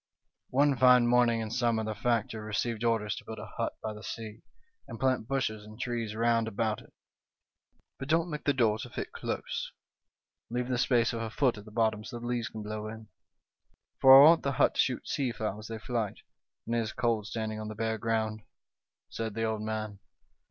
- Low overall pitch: Yes, low, 115 Hz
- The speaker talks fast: Yes, fast, 215 wpm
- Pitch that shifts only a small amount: Yes, narrow, 2.1 semitones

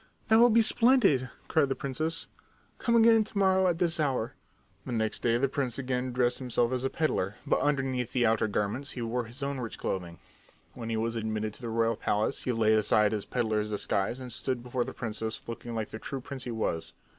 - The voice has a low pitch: Yes, low, 125 Hz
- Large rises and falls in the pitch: No, average, 3.9 semitones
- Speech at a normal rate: No, fast, 215 wpm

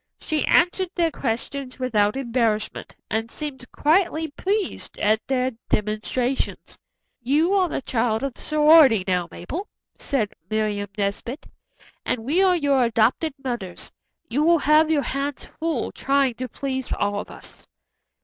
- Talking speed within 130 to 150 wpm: Yes, average, 140 wpm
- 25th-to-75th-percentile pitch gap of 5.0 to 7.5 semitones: Yes, wide, 5.5 semitones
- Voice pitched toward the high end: Yes, very high, 265 Hz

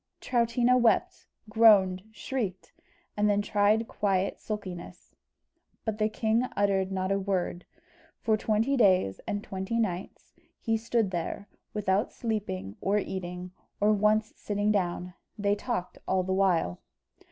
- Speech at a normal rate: No, slow, 130 wpm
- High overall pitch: Yes, high, 205 Hz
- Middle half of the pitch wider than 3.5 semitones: No, narrow, 2.6 semitones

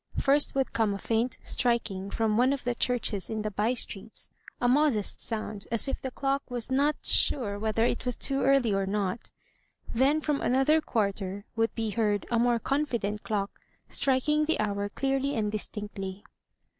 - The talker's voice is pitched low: No, high, 230 Hz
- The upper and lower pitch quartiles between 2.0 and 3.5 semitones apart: No, average, 4.4 semitones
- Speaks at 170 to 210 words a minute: Yes, average, 175 wpm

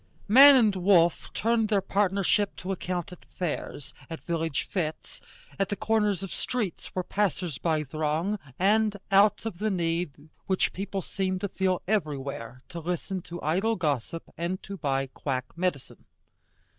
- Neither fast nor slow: Yes, average, 155 wpm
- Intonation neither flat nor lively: Yes, average, 3.9 semitones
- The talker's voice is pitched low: No, medium, 185 Hz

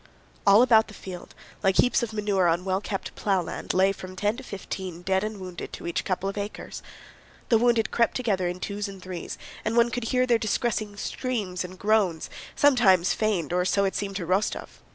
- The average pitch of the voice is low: No, high, 200 Hz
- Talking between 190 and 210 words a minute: Yes, average, 195 wpm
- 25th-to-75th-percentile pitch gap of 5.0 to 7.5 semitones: No, average, 3.0 semitones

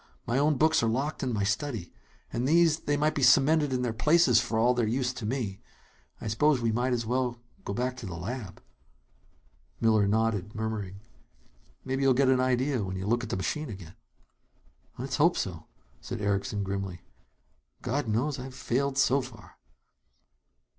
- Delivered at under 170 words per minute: No, average, 175 wpm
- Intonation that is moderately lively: Yes, average, 4.1 semitones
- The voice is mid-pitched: No, low, 125 Hz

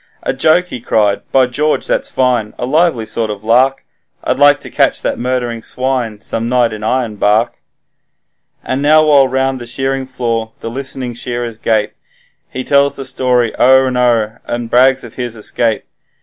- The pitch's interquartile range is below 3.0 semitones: Yes, narrow, 2.6 semitones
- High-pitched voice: No, low, 125 Hz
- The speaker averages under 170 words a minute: No, average, 175 wpm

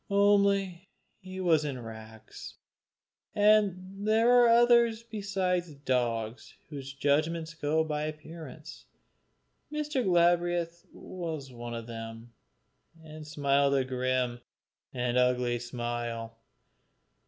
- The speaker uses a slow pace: Yes, slow, 100 wpm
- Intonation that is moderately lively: No, wide, 7.1 semitones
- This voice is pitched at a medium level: Yes, medium, 155 Hz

